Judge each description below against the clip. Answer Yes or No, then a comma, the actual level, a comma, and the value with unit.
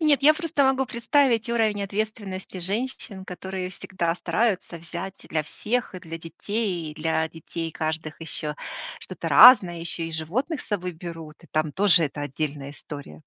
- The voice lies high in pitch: No, medium, 180 Hz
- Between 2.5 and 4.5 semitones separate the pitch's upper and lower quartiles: No, wide, 5.4 semitones